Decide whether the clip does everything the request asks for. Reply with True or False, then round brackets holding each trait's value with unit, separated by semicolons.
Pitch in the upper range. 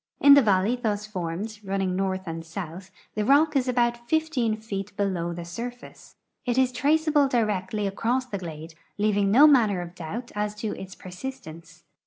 True (210 Hz)